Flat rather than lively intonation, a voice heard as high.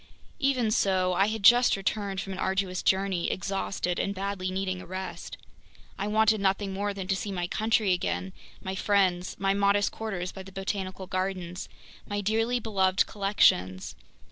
Yes: narrow, 1.6 semitones; high, 195 Hz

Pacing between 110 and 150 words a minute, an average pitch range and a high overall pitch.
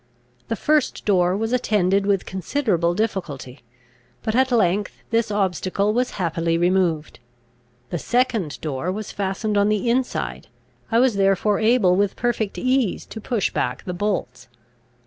Yes: average, 145 wpm; average, 4.2 semitones; high, 200 Hz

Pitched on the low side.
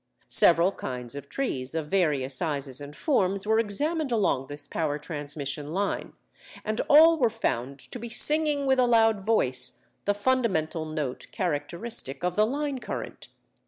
No: medium, 185 Hz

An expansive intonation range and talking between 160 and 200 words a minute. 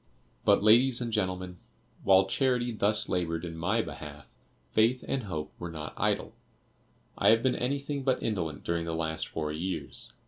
Yes: wide, 6.3 semitones; average, 165 wpm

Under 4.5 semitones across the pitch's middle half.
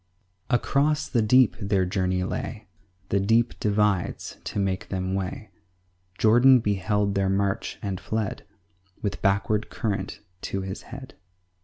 Yes: average, 2.7 semitones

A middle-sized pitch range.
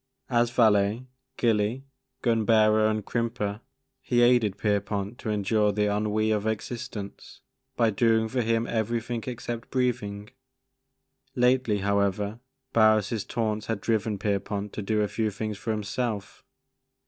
No: narrow, 2.2 semitones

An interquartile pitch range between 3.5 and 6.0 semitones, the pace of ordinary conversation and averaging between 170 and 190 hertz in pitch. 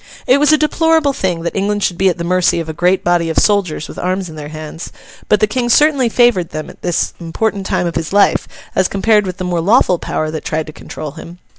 No: average, 4.2 semitones; fast, 250 wpm; medium, 185 Hz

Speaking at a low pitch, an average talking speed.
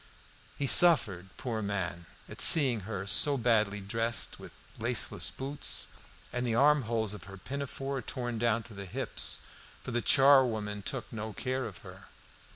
Yes: low, 115 Hz; average, 160 wpm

